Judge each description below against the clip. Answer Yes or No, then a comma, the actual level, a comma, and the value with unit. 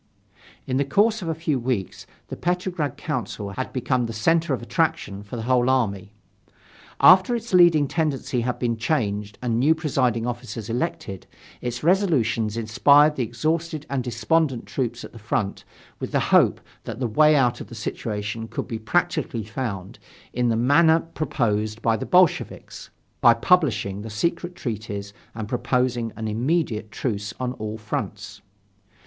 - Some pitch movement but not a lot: No, wide, 5.7 semitones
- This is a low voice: Yes, low, 125 Hz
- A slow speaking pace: No, average, 160 wpm